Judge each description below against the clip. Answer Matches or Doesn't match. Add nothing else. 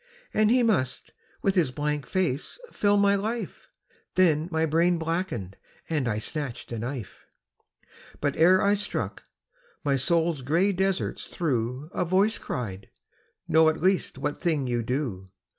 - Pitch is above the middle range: Doesn't match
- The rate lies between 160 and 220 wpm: Doesn't match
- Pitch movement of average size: Doesn't match